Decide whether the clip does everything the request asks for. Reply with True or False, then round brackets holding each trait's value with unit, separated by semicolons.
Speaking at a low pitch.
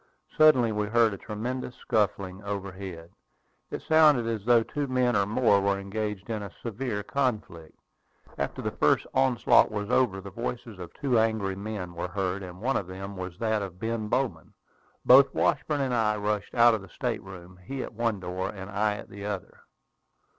True (105 Hz)